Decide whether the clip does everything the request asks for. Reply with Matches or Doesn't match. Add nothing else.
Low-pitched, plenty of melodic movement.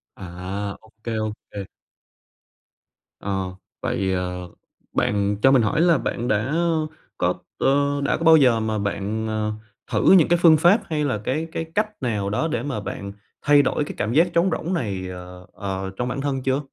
Matches